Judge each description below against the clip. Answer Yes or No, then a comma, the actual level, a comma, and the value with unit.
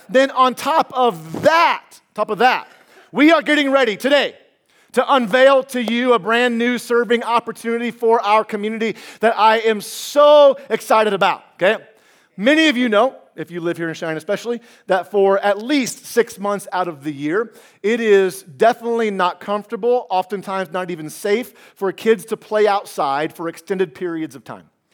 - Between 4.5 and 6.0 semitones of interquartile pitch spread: No, average, 4.1 semitones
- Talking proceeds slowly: No, average, 175 wpm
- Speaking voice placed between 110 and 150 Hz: No, high, 225 Hz